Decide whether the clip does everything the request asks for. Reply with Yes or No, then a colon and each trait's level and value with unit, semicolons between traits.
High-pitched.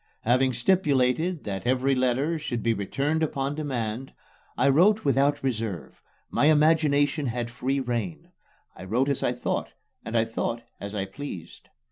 No: low, 130 Hz